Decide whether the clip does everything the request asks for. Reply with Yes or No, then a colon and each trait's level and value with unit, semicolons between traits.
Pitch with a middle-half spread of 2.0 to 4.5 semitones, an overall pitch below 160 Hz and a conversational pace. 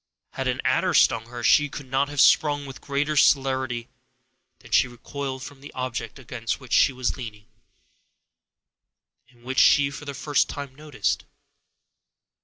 Yes: narrow, 2.4 semitones; low, 135 Hz; average, 155 wpm